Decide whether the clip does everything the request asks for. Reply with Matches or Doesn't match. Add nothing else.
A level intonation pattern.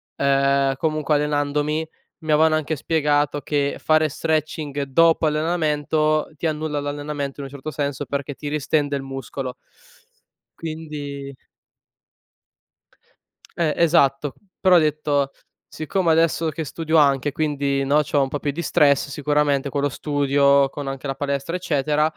Matches